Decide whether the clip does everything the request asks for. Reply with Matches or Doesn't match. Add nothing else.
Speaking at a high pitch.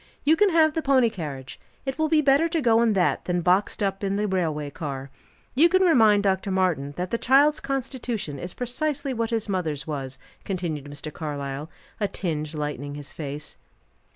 Matches